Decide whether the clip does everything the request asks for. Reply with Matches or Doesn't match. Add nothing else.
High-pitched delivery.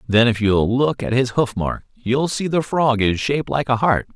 Doesn't match